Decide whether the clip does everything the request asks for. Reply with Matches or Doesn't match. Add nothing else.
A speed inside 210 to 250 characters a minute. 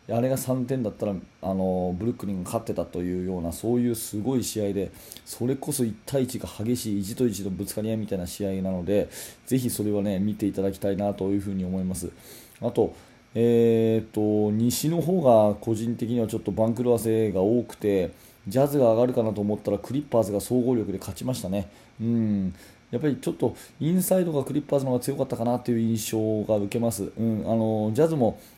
Doesn't match